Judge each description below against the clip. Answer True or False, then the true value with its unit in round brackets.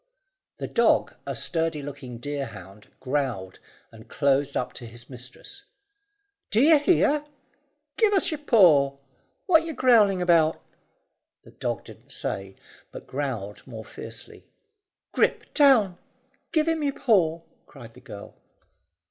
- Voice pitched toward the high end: False (150 Hz)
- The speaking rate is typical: False (125 wpm)